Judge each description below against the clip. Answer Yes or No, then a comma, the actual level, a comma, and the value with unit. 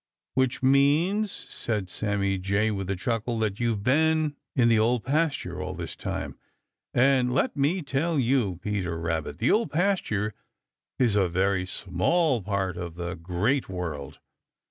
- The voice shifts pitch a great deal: Yes, wide, 6.6 semitones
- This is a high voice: No, low, 110 Hz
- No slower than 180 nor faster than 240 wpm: No, average, 150 wpm